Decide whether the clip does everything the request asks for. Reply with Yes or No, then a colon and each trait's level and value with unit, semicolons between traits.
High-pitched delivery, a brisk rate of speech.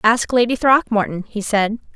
No: high, 225 Hz; average, 155 wpm